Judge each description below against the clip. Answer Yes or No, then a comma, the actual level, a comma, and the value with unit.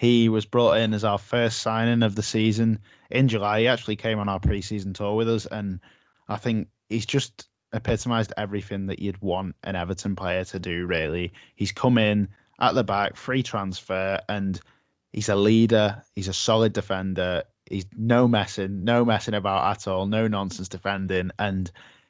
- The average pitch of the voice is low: Yes, low, 105 Hz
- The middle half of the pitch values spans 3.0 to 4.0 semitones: No, narrow, 2.6 semitones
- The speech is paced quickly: No, average, 180 wpm